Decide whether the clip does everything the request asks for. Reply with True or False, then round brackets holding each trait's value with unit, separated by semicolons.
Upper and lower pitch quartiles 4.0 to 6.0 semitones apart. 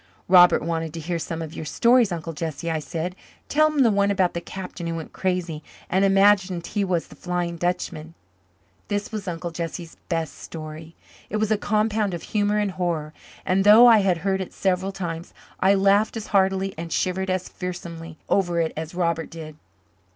False (3.0 semitones)